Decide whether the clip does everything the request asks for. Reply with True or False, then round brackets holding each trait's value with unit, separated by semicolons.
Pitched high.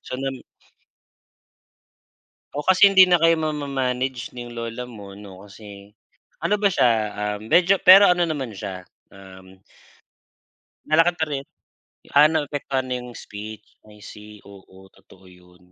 False (125 Hz)